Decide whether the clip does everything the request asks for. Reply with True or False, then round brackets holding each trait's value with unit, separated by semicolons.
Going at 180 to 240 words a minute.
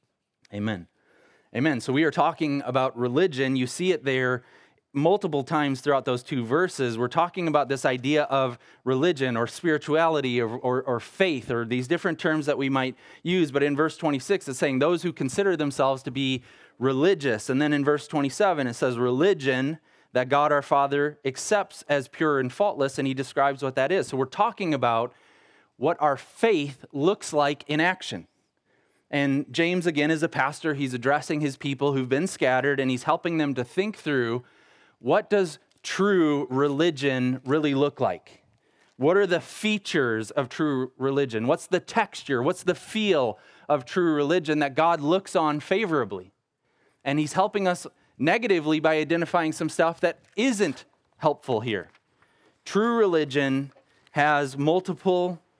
False (165 wpm)